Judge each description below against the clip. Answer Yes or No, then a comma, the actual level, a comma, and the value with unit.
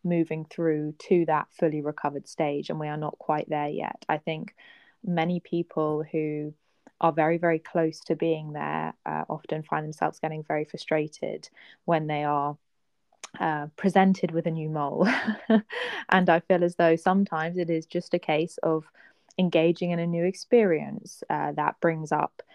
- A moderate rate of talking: Yes, average, 170 wpm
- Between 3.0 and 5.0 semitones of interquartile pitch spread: No, narrow, 2.4 semitones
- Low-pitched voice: No, medium, 165 Hz